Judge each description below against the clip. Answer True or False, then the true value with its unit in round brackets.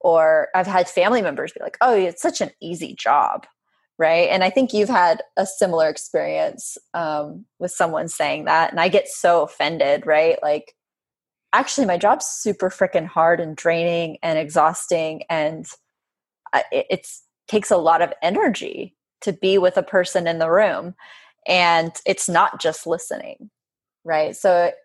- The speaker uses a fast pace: False (160 wpm)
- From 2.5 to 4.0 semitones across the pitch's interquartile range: True (3.7 semitones)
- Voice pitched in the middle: True (175 Hz)